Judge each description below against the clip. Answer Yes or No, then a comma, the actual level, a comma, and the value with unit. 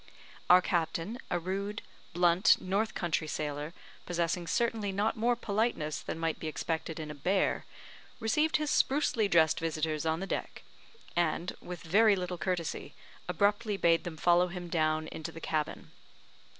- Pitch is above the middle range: No, medium, 175 Hz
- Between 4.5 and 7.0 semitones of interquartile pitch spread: No, average, 4.0 semitones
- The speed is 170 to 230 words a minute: No, average, 150 wpm